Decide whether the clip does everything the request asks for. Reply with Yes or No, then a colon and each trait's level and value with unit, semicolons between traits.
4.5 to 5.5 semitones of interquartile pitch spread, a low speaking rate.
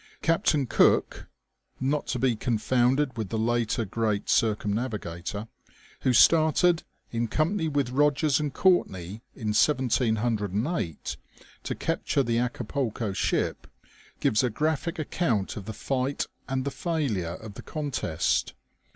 Yes: average, 5.1 semitones; slow, 125 wpm